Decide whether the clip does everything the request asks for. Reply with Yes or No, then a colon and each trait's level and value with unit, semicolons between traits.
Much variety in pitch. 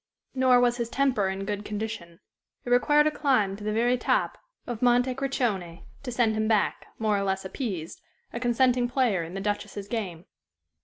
No: average, 3.9 semitones